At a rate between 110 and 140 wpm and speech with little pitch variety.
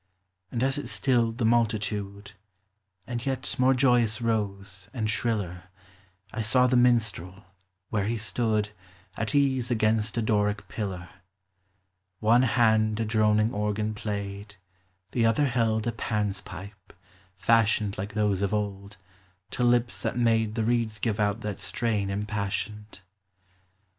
Yes: slow, 135 wpm; narrow, 2.3 semitones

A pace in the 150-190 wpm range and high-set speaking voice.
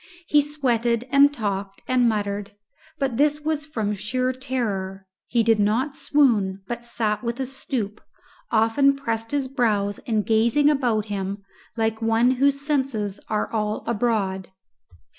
No: average, 140 wpm; high, 230 Hz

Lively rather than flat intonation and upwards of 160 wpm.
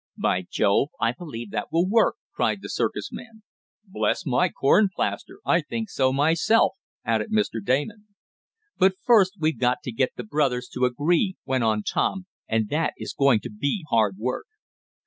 Yes: wide, 7.4 semitones; average, 170 wpm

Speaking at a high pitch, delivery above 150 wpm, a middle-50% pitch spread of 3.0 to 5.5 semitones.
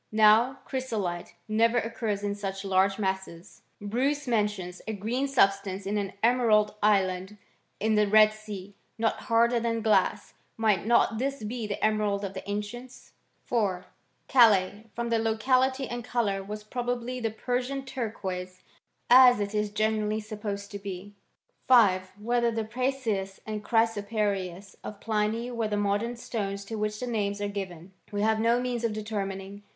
No: high, 215 Hz; average, 160 wpm; narrow, 2.6 semitones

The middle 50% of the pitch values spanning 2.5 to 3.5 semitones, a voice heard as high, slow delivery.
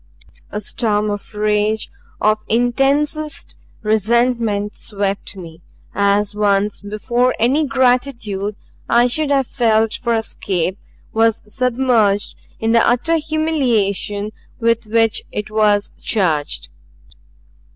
Yes: average, 3.2 semitones; high, 220 Hz; slow, 105 wpm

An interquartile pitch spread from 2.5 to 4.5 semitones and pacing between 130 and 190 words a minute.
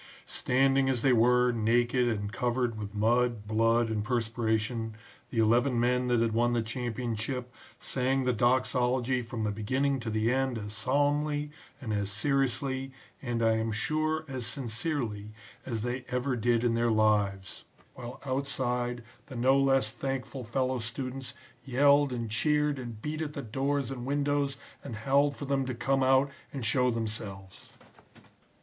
Yes: average, 3.0 semitones; average, 160 wpm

